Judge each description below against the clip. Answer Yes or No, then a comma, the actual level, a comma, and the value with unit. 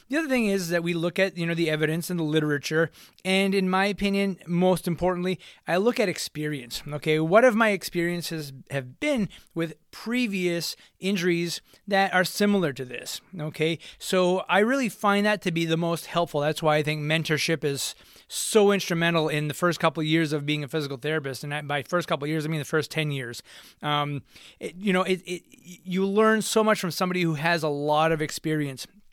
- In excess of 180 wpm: Yes, fast, 205 wpm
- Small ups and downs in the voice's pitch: No, average, 3.6 semitones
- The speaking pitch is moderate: Yes, medium, 170 Hz